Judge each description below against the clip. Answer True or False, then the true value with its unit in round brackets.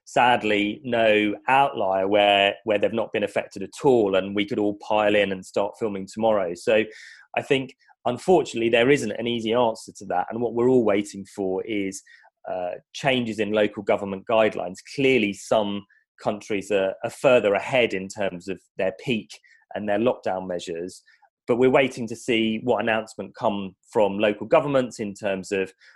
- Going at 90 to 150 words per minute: False (175 wpm)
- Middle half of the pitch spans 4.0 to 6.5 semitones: False (3.2 semitones)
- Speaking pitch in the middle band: False (105 Hz)